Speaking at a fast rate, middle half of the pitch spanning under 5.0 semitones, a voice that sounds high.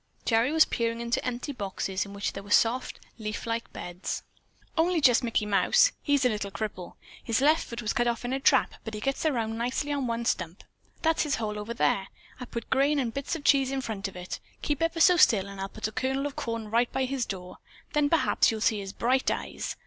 Yes: fast, 235 wpm; average, 4.4 semitones; high, 235 Hz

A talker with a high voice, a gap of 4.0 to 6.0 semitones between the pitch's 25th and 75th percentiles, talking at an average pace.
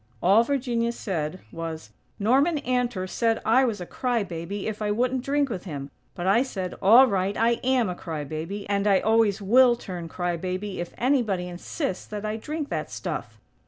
Yes: high, 205 Hz; average, 5.0 semitones; average, 190 wpm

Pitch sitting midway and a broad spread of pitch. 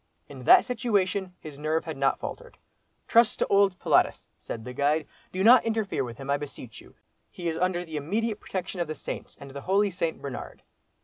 Yes: medium, 170 Hz; wide, 6.0 semitones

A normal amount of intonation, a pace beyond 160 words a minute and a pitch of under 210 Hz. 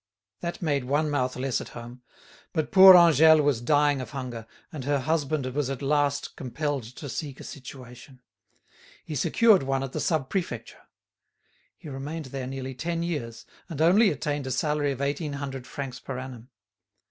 Yes: average, 3.0 semitones; average, 170 wpm; medium, 140 Hz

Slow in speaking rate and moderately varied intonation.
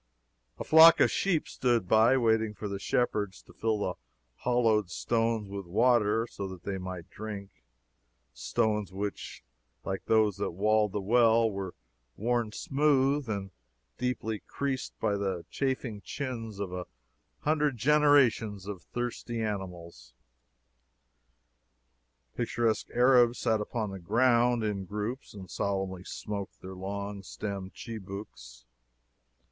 Yes: slow, 125 wpm; average, 3.6 semitones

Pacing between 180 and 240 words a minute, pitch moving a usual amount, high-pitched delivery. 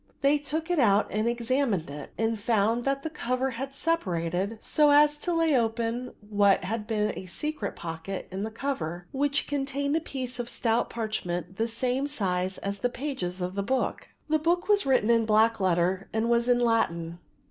No: average, 190 wpm; wide, 5.7 semitones; high, 230 Hz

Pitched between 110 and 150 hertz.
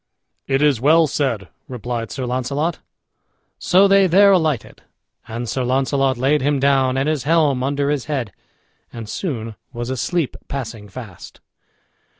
Yes: low, 135 Hz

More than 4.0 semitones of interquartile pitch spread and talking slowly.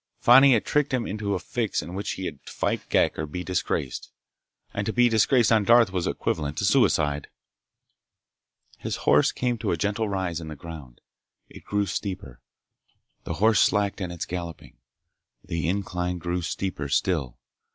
No: average, 4.5 semitones; average, 170 wpm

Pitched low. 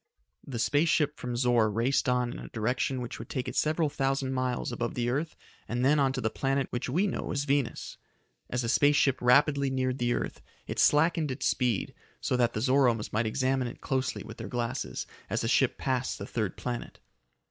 Yes: low, 130 Hz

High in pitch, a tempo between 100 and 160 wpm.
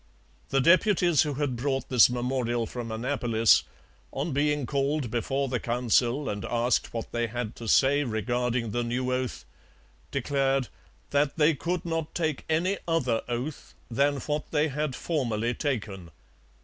No: low, 130 Hz; average, 150 wpm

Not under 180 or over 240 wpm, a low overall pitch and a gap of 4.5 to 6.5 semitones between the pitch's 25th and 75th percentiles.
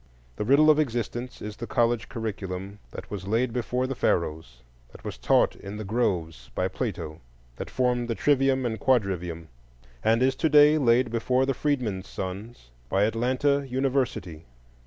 No: average, 160 wpm; low, 115 Hz; average, 5.0 semitones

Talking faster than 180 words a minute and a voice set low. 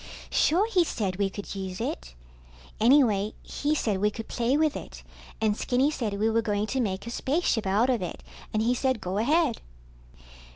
No: average, 190 wpm; high, 225 Hz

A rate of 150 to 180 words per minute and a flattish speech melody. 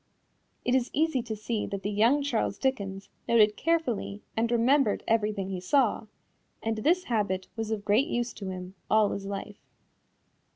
No: average, 165 wpm; average, 3.6 semitones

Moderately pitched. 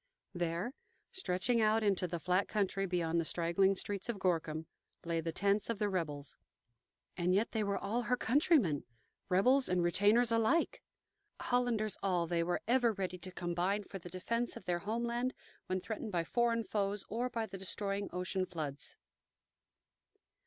No: high, 195 Hz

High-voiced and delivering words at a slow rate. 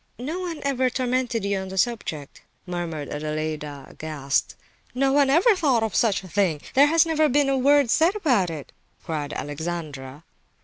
No: high, 215 Hz; average, 170 wpm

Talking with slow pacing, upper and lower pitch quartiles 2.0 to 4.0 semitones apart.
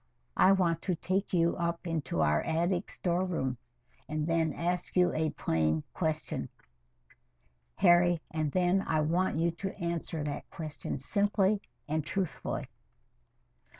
Yes: slow, 130 wpm; average, 2.8 semitones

